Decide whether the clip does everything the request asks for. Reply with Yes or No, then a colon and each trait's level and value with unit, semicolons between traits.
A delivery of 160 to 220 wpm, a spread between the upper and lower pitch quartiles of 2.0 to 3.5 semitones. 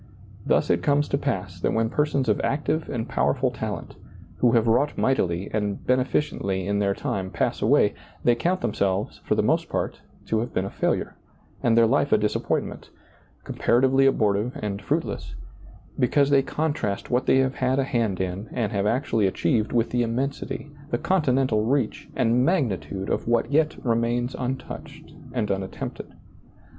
No: average, 170 wpm; average, 4.6 semitones